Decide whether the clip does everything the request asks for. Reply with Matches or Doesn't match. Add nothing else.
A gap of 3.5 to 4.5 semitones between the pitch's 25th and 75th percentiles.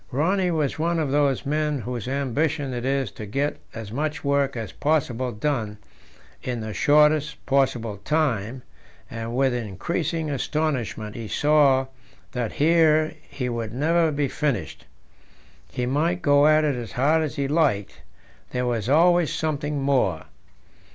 Matches